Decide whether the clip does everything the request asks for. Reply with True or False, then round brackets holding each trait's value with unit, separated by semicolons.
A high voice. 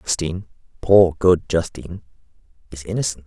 False (85 Hz)